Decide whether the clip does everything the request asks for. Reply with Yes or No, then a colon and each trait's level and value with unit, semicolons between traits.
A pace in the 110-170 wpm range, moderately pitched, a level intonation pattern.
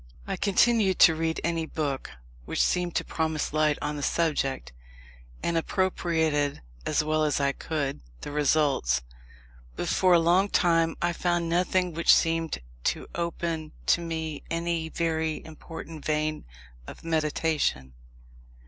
Yes: average, 140 wpm; medium, 160 Hz; narrow, 1.9 semitones